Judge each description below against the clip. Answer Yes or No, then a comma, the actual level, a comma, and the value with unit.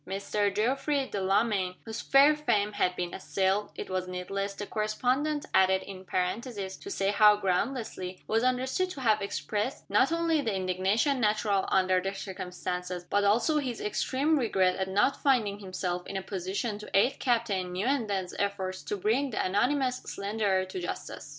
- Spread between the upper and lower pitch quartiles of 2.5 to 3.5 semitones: No, average, 4.8 semitones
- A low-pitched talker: No, high, 205 Hz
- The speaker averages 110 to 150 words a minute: No, average, 165 wpm